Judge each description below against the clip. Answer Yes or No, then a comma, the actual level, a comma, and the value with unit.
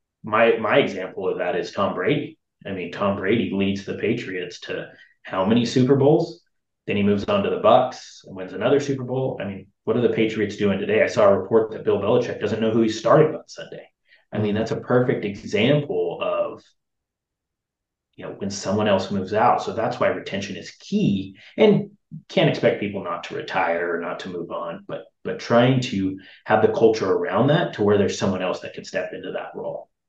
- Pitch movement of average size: No, wide, 5.7 semitones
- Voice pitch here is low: Yes, low, 110 Hz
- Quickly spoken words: Yes, fast, 210 wpm